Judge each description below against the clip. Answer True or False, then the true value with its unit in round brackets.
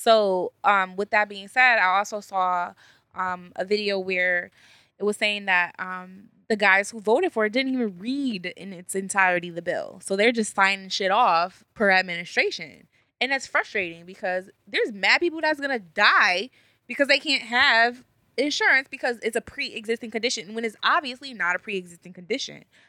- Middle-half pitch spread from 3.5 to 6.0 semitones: True (4.8 semitones)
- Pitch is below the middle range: False (210 Hz)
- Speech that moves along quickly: False (180 wpm)